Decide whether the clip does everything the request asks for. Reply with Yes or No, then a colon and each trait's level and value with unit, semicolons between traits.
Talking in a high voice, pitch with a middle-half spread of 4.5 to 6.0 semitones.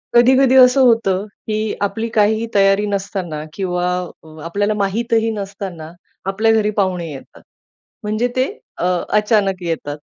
No: high, 205 Hz; average, 3.3 semitones